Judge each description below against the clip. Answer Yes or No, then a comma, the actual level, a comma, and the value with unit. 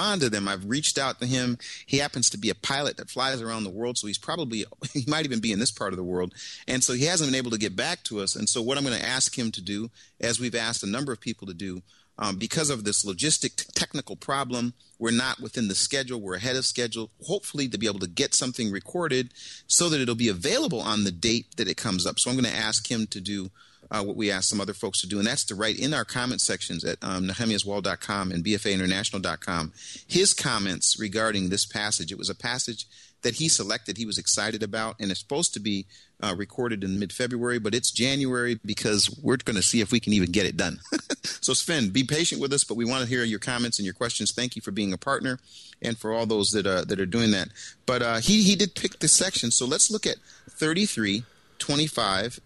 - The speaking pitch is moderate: No, low, 115 Hz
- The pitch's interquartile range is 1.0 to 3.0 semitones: No, average, 3.9 semitones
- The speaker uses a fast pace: Yes, fast, 245 wpm